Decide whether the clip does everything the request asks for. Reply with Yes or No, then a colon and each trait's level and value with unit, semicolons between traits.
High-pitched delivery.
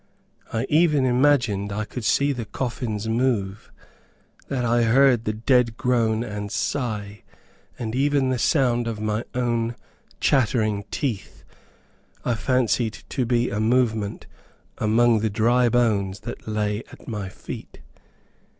No: low, 115 Hz